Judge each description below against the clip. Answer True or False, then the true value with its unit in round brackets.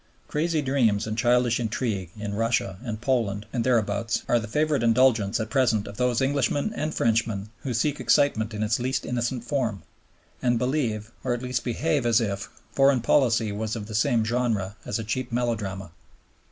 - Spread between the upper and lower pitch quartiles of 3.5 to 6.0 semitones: False (3.0 semitones)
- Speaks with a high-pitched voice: False (115 Hz)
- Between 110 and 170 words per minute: False (180 wpm)